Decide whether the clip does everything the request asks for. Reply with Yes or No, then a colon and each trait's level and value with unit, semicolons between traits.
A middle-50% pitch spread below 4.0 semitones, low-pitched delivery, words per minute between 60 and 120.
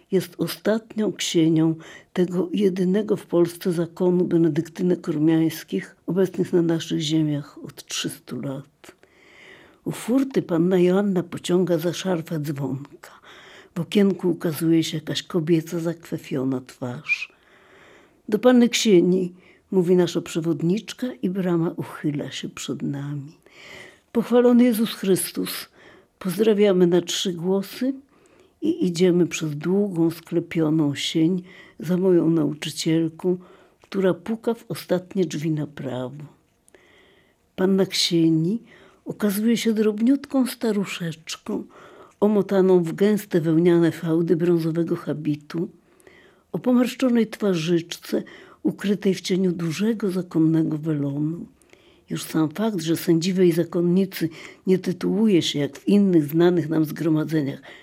No: average, 3.2 semitones; medium, 175 Hz; slow, 110 wpm